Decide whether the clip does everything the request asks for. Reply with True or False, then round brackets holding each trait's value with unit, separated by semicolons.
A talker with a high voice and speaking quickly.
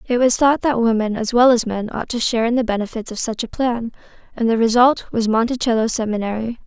True (230 Hz; 225 wpm)